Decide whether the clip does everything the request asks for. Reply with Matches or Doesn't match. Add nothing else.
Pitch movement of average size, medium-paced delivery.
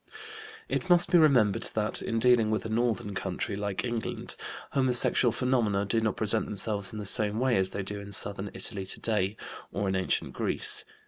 Matches